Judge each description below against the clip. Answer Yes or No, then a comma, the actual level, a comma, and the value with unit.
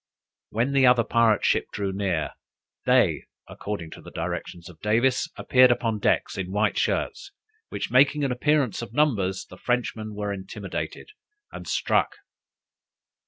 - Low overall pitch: Yes, low, 110 Hz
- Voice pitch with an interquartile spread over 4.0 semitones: Yes, average, 4.6 semitones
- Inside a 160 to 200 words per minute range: No, average, 145 wpm